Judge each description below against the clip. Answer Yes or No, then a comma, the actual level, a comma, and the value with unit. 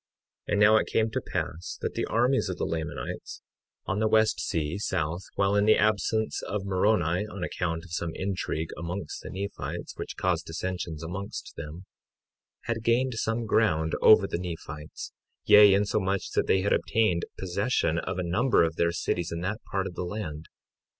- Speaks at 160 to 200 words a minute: Yes, average, 180 wpm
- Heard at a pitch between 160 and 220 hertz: No, very low, 95 Hz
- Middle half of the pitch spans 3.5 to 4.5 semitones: Yes, average, 4.0 semitones